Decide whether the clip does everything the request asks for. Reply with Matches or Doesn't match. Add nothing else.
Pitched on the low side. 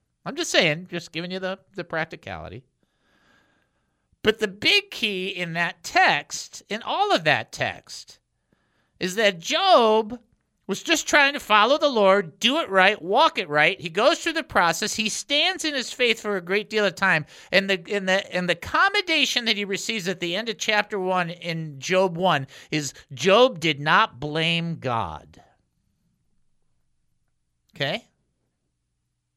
Doesn't match